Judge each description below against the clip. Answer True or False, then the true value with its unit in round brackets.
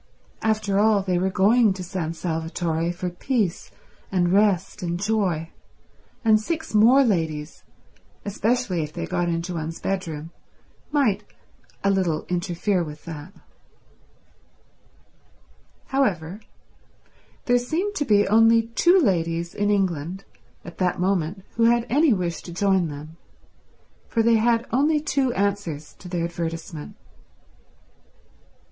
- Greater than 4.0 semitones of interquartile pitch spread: True (4.7 semitones)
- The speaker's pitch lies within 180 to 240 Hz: True (190 Hz)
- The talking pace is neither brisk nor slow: False (125 wpm)